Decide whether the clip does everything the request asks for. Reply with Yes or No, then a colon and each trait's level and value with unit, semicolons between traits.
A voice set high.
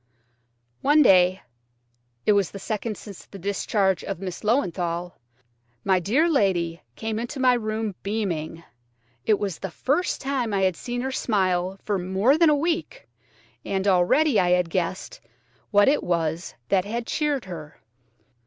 Yes: high, 195 Hz